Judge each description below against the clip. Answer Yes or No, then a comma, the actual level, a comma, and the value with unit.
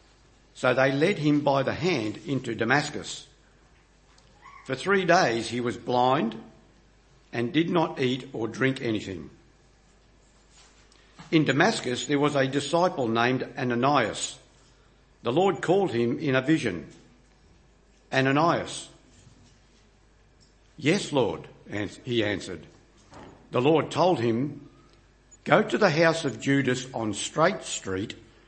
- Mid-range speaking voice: No, low, 130 Hz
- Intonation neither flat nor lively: Yes, average, 4.1 semitones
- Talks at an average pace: No, slow, 115 wpm